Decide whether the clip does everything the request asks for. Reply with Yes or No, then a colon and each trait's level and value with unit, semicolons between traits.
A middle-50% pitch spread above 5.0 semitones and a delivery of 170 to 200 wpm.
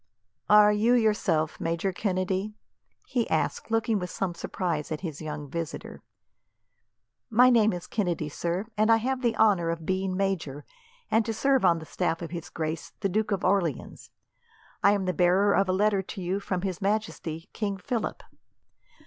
No: average, 4.0 semitones; average, 175 wpm